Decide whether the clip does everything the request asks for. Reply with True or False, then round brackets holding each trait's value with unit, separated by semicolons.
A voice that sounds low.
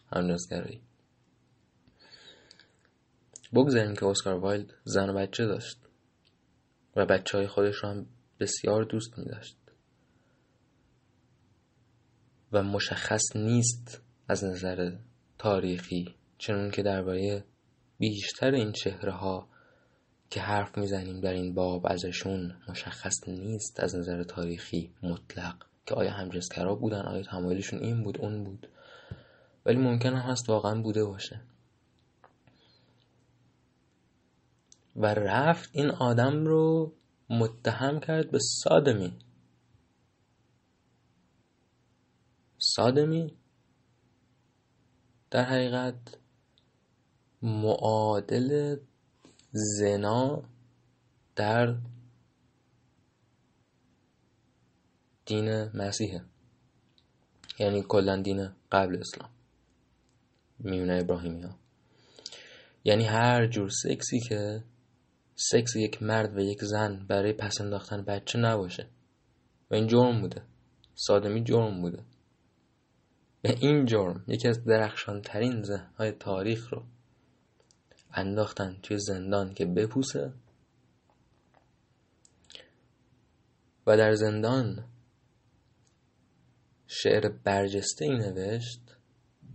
True (110 Hz)